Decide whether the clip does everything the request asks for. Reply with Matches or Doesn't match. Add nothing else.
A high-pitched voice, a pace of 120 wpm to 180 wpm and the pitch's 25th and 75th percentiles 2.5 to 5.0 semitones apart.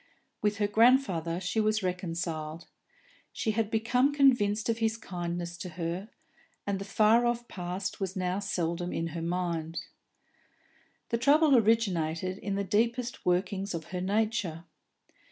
Matches